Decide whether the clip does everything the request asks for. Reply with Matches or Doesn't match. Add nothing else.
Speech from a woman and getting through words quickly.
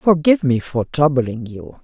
Doesn't match